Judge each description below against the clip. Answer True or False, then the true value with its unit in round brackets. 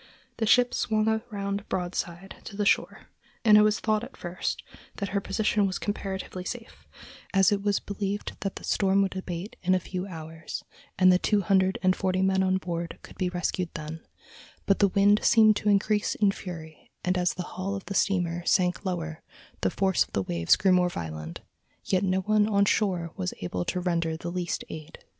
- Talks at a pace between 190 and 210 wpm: True (200 wpm)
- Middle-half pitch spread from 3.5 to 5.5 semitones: False (2.5 semitones)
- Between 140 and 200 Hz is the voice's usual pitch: True (190 Hz)